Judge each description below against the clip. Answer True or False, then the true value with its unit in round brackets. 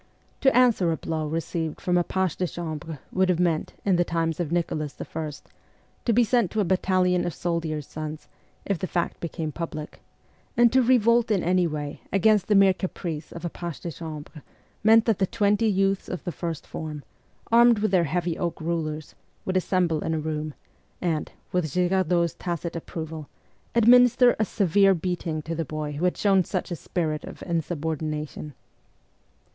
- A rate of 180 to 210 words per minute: True (185 wpm)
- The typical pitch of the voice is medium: True (175 Hz)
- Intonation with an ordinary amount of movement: True (3.4 semitones)